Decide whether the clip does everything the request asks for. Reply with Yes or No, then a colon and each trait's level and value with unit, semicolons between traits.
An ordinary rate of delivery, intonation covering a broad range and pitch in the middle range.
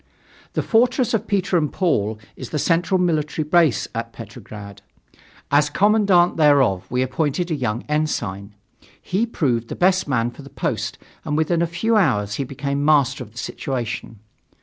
Yes: average, 165 wpm; wide, 6.6 semitones; medium, 150 Hz